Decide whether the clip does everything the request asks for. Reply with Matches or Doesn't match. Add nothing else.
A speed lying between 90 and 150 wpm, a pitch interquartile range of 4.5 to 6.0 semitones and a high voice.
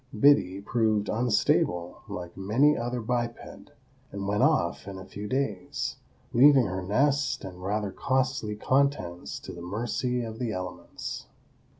Doesn't match